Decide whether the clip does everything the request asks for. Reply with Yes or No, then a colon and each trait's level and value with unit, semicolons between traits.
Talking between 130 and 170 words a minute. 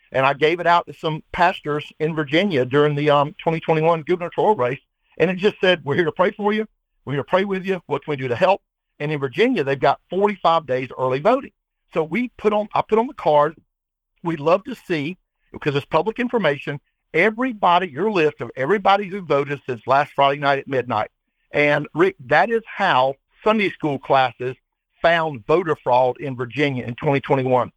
No: average, 195 wpm